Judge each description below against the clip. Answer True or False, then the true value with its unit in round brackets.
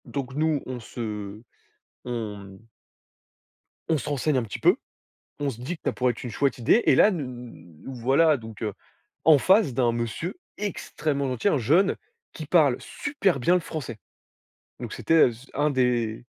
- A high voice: False (130 Hz)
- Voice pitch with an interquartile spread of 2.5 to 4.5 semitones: False (4.9 semitones)